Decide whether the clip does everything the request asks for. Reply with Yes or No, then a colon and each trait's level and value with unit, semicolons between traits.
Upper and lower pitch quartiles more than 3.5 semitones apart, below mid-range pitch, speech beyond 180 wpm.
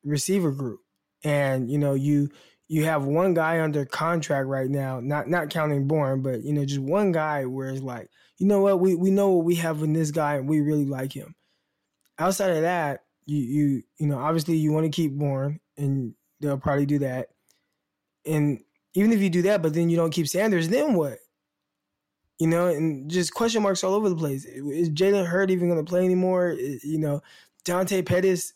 No: average, 4.0 semitones; medium, 155 Hz; fast, 205 wpm